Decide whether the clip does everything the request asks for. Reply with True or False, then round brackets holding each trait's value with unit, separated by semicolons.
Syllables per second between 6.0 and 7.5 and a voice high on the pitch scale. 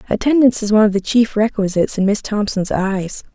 True (6.2 syllables/s; 210 Hz)